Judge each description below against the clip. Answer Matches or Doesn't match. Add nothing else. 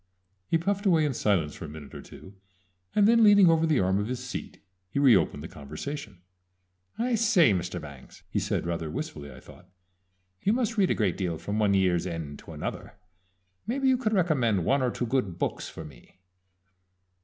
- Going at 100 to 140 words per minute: Doesn't match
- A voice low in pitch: Matches